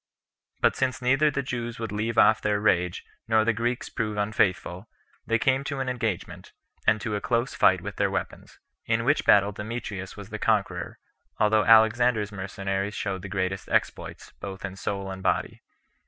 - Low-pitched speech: Yes, low, 105 Hz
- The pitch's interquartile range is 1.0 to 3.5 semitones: Yes, average, 2.9 semitones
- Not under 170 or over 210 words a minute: Yes, average, 175 wpm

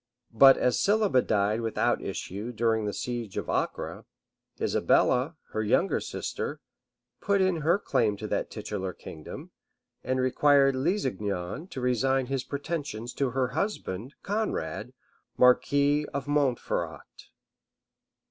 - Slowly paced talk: Yes, slow, 125 wpm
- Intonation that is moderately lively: Yes, average, 4.6 semitones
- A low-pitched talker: Yes, low, 130 Hz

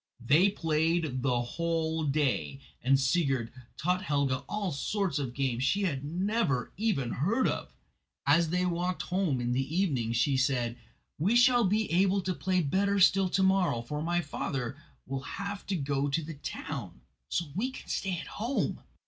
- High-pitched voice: No, medium, 160 Hz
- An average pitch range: No, wide, 5.8 semitones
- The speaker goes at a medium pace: Yes, average, 170 wpm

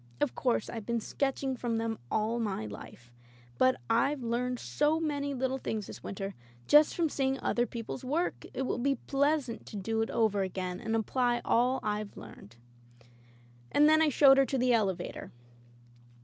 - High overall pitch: Yes, high, 240 Hz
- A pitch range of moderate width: Yes, average, 3.8 semitones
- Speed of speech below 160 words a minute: No, average, 175 wpm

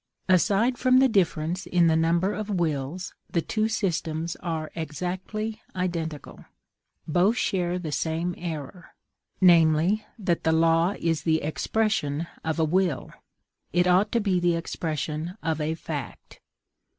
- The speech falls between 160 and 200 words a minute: No, average, 140 wpm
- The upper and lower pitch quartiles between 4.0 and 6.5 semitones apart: No, average, 2.9 semitones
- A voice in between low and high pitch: Yes, medium, 170 Hz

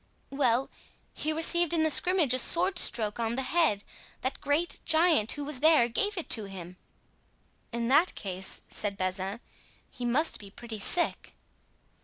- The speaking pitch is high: Yes, very high, 260 Hz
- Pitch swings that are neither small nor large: No, wide, 7.2 semitones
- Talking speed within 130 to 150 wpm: No, average, 160 wpm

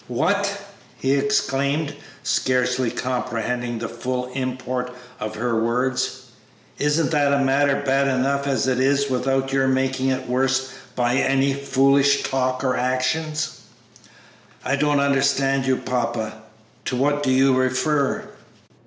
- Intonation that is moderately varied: No, narrow, 1.6 semitones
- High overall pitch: No, low, 135 Hz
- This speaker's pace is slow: Yes, slow, 125 wpm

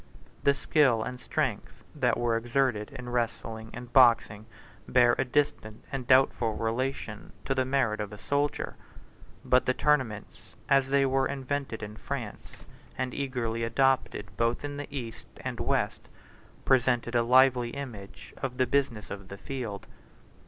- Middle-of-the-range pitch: No, low, 125 Hz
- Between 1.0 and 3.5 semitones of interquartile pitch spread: Yes, average, 2.9 semitones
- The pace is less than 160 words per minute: Yes, average, 150 wpm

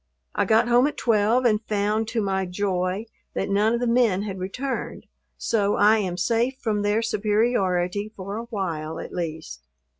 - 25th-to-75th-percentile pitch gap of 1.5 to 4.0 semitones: Yes, average, 3.2 semitones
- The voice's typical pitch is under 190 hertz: No, high, 210 Hz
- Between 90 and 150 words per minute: No, average, 175 wpm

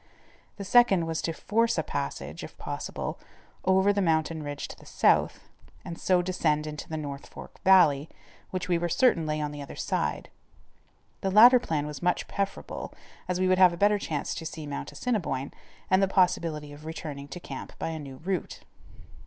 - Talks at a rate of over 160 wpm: Yes, average, 190 wpm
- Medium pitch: Yes, medium, 170 Hz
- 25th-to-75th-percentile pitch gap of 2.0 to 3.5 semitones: No, average, 4.0 semitones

